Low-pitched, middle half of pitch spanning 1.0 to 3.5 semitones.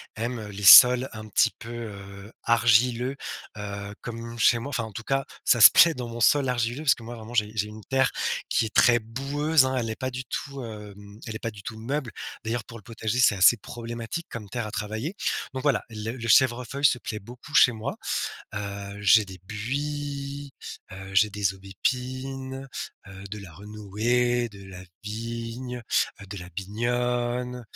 Yes: low, 115 Hz; average, 3.2 semitones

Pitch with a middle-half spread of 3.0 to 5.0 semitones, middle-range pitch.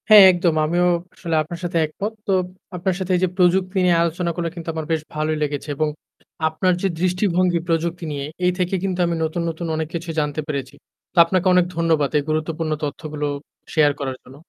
No: narrow, 2.6 semitones; medium, 170 Hz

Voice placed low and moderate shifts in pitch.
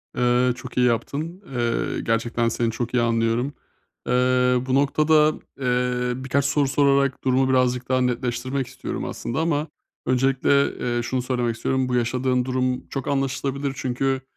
No: low, 130 Hz; narrow, 1.8 semitones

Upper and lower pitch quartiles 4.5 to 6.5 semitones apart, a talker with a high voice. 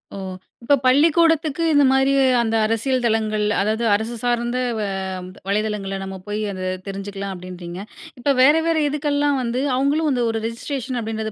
Yes: average, 4.8 semitones; high, 235 Hz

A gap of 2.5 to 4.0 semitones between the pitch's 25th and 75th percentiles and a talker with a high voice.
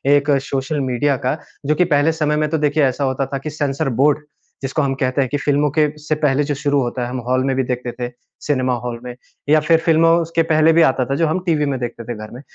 No: average, 2.9 semitones; medium, 140 Hz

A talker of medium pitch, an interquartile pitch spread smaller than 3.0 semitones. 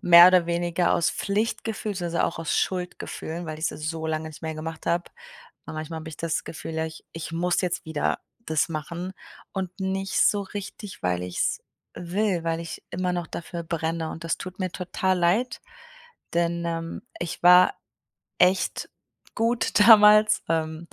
Yes: medium, 170 Hz; narrow, 2.4 semitones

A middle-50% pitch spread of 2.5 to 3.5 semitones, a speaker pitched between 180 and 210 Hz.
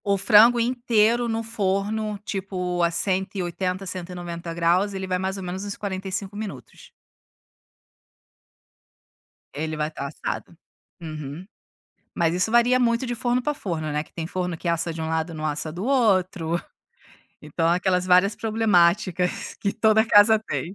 No: average, 3.9 semitones; medium, 185 Hz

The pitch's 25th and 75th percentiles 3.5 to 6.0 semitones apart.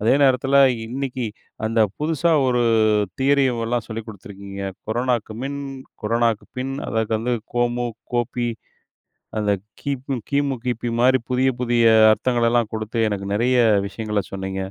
No: average, 2.8 semitones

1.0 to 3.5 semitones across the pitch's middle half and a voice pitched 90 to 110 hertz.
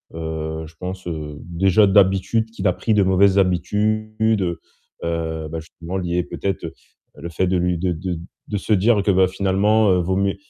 Yes: average, 2.8 semitones; very low, 95 Hz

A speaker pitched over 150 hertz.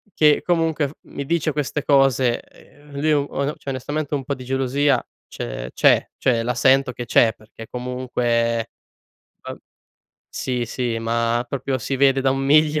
No: low, 135 Hz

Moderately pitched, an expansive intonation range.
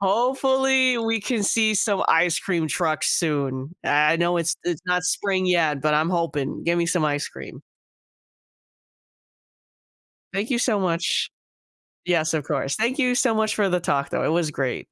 Yes: medium, 175 Hz; wide, 5.7 semitones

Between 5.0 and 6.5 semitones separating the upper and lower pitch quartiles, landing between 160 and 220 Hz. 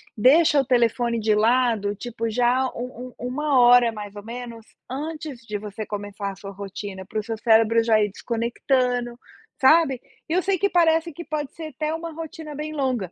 No: wide, 5.4 semitones; high, 245 Hz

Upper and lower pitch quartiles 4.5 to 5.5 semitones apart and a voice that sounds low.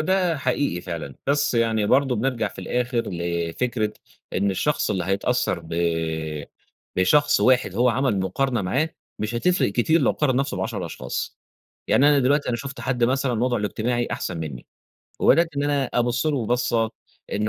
Yes: average, 5.1 semitones; low, 120 Hz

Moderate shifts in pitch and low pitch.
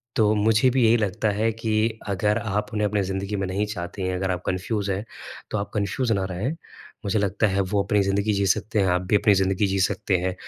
No: narrow, 2.0 semitones; low, 100 Hz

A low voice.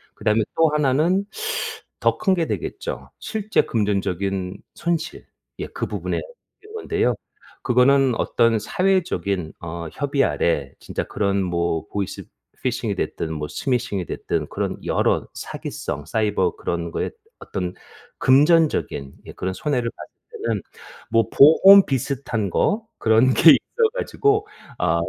Yes: low, 115 Hz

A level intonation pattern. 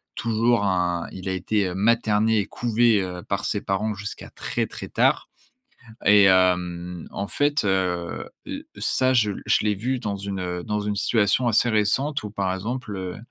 No: average, 3.3 semitones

